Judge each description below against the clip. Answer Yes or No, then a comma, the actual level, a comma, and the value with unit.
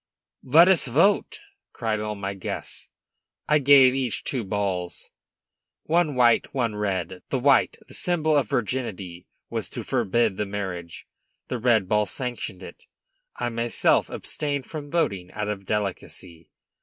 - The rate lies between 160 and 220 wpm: No, average, 140 wpm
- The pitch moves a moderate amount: No, wide, 5.8 semitones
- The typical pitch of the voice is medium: No, low, 115 Hz